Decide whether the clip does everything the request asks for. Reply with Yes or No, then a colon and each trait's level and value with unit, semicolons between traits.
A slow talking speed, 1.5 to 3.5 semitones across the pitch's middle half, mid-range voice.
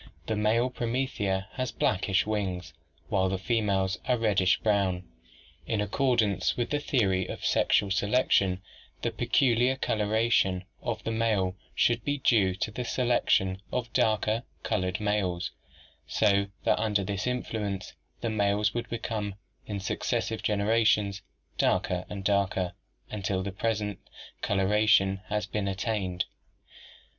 No: slow, 130 wpm; average, 2.9 semitones; low, 105 Hz